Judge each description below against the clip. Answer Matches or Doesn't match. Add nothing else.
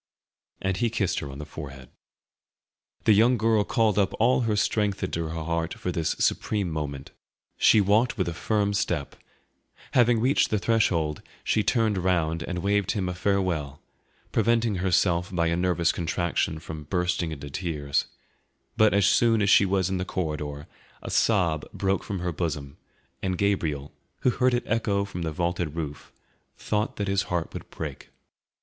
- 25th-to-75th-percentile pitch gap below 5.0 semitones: Matches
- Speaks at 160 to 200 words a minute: Matches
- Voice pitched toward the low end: Matches